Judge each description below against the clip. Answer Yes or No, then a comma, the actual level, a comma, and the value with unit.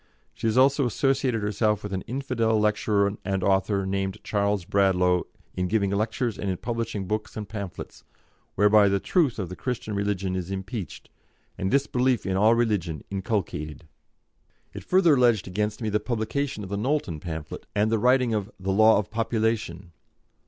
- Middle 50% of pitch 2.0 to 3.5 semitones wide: Yes, average, 3.0 semitones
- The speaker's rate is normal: Yes, average, 165 wpm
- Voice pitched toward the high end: No, low, 105 Hz